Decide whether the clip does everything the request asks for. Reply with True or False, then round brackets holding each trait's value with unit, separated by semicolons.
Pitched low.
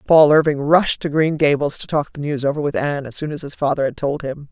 False (145 Hz)